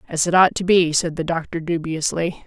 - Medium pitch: Yes, medium, 165 Hz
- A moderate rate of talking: No, fast, 220 wpm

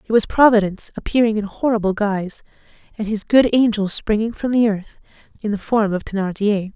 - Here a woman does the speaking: Yes, female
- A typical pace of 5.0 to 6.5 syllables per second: Yes, 5.7 syllables/s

